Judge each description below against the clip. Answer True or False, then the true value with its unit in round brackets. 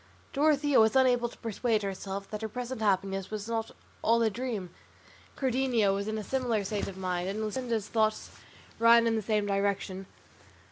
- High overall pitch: True (220 Hz)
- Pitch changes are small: False (3.2 semitones)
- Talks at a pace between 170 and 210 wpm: True (175 wpm)